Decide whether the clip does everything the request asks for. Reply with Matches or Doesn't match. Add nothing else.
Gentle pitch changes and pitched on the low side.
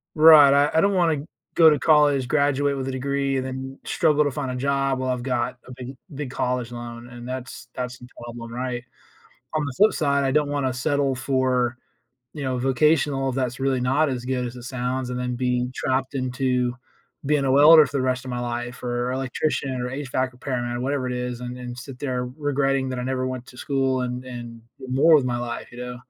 Matches